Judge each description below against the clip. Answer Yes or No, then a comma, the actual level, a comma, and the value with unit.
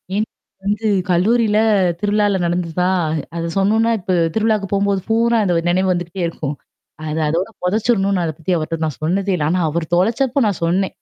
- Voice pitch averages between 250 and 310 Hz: No, high, 190 Hz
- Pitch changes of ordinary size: Yes, average, 3.4 semitones